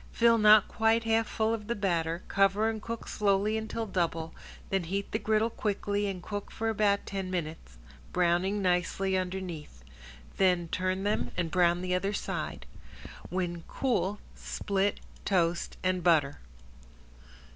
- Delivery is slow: No, average, 145 wpm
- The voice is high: Yes, high, 195 Hz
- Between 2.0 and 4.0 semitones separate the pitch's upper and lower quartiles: Yes, average, 3.1 semitones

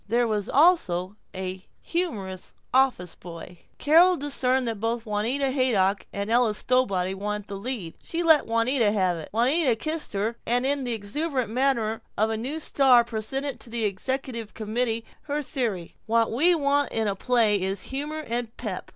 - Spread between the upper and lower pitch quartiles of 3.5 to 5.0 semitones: Yes, average, 4.5 semitones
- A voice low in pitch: No, high, 230 Hz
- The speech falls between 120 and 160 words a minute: No, average, 170 wpm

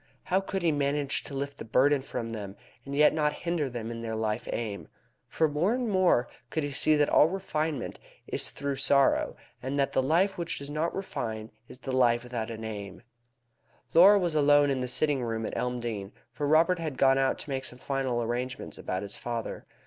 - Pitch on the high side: No, low, 135 Hz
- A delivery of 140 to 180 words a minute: No, fast, 205 wpm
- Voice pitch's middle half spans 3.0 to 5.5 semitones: Yes, average, 4.5 semitones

